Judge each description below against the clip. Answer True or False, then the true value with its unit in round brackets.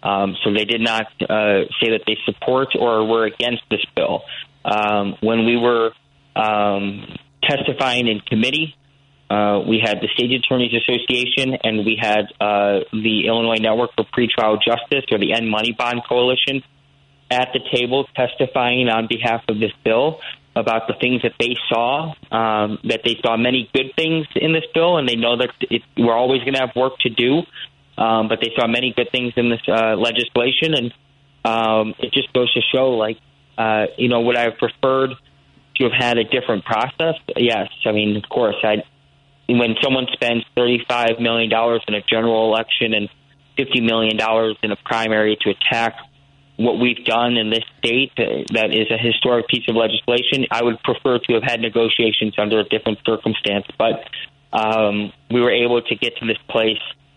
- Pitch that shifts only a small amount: True (2.3 semitones)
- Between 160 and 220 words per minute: True (185 wpm)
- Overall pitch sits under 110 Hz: False (115 Hz)